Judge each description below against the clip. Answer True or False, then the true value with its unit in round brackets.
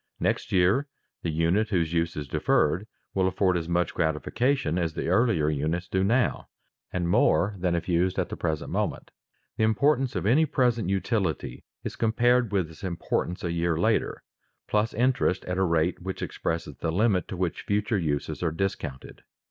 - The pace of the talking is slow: False (175 wpm)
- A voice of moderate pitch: False (90 Hz)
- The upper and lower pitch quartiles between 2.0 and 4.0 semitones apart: False (4.4 semitones)